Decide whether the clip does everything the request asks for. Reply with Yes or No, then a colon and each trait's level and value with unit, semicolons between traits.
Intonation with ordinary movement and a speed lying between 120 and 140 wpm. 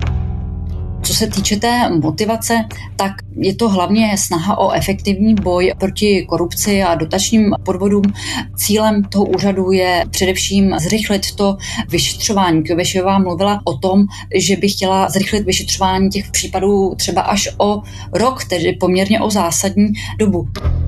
Yes: average, 3.1 semitones; average, 130 wpm